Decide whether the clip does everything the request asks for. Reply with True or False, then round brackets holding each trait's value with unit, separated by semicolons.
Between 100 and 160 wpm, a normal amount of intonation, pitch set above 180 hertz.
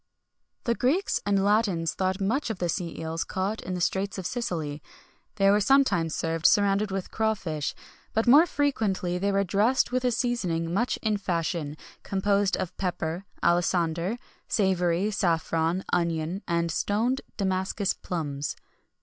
True (150 wpm; 3.9 semitones; 190 Hz)